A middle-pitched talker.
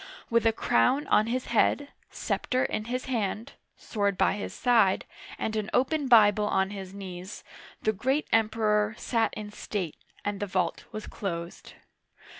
No: high, 215 Hz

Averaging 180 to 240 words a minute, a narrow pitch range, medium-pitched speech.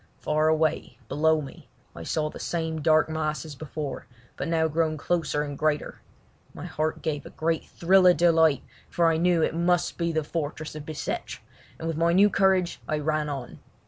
Yes: average, 190 wpm; narrow, 1.6 semitones; medium, 160 Hz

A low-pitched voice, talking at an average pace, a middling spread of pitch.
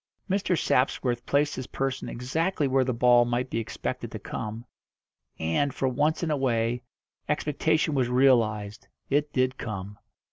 Yes: low, 130 Hz; average, 150 wpm; average, 3.4 semitones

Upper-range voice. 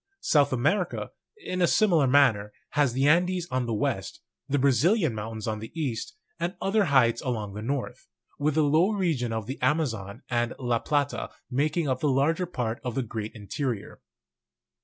No: low, 135 Hz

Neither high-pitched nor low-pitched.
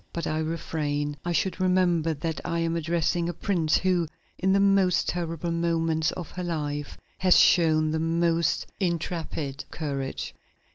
Yes: medium, 165 Hz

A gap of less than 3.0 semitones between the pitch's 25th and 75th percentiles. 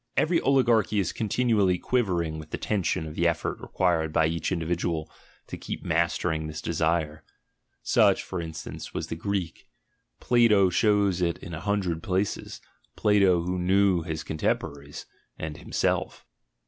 No: average, 3.8 semitones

